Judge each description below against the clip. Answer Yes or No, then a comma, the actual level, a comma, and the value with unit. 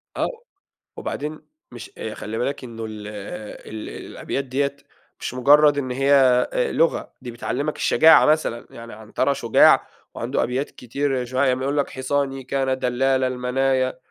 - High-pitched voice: No, low, 130 Hz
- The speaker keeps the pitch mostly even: Yes, narrow, 2.2 semitones